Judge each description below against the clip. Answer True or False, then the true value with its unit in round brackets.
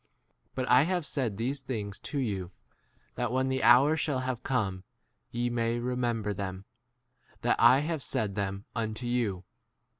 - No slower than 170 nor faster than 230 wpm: False (160 wpm)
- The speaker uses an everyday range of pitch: True (4.0 semitones)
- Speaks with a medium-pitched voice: False (120 Hz)